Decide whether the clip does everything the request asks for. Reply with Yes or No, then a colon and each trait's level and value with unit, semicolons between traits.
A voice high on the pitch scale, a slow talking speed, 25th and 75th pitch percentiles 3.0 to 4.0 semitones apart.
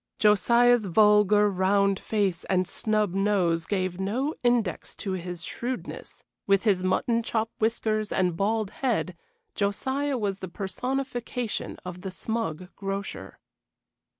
Yes: high, 205 Hz; slow, 125 wpm; average, 3.4 semitones